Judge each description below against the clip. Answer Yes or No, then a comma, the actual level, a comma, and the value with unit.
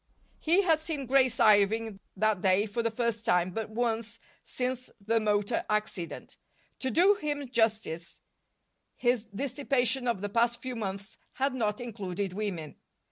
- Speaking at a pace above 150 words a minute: No, average, 145 wpm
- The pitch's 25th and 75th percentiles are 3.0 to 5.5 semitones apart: Yes, average, 3.8 semitones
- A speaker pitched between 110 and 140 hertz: No, high, 225 Hz